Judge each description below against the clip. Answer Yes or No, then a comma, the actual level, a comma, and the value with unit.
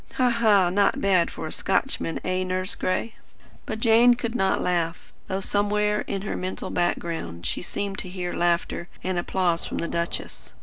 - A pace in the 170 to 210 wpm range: Yes, average, 175 wpm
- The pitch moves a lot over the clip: No, average, 3.0 semitones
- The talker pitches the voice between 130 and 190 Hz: Yes, medium, 185 Hz